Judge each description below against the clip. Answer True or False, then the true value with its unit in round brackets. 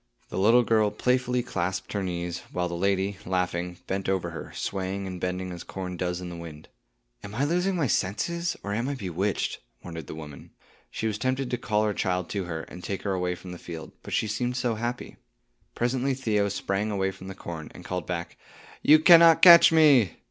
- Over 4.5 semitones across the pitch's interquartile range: True (5.3 semitones)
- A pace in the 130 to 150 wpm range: False (205 wpm)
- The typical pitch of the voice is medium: False (95 Hz)